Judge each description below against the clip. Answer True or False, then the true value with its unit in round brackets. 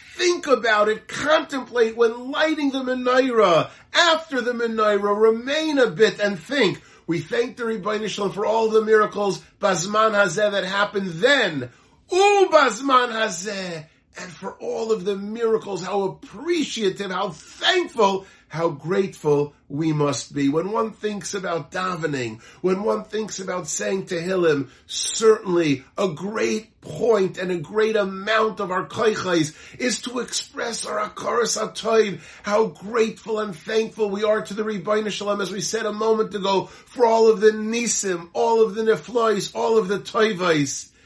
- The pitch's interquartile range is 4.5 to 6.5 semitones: False (3.1 semitones)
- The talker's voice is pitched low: False (215 Hz)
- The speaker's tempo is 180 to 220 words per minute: False (155 wpm)